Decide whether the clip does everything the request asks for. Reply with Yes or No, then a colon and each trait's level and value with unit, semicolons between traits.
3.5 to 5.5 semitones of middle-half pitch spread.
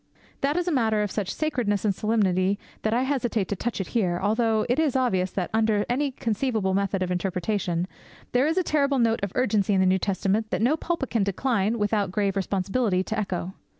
Yes: average, 4.3 semitones